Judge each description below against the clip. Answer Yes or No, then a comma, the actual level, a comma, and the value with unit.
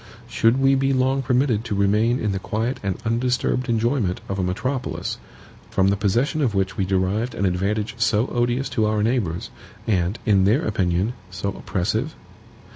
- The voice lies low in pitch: Yes, low, 110 Hz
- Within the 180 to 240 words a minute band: No, average, 170 wpm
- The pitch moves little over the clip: No, average, 4.2 semitones